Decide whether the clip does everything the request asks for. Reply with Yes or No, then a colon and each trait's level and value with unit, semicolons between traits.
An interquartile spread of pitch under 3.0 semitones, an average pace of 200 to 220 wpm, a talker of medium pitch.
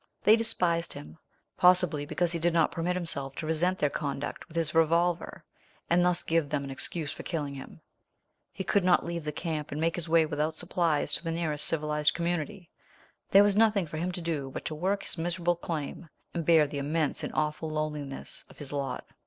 Yes: narrow, 2.6 semitones; fast, 205 wpm; medium, 165 Hz